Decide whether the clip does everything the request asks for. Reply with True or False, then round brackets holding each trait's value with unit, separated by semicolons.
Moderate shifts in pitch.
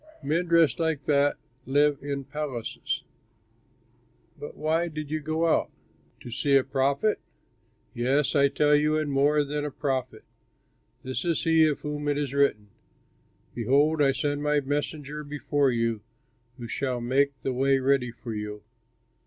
False (2.1 semitones)